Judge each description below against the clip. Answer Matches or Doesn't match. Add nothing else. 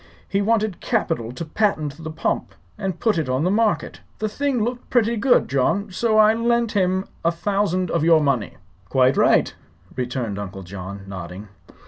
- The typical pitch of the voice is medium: Matches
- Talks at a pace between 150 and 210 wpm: Matches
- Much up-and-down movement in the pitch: Matches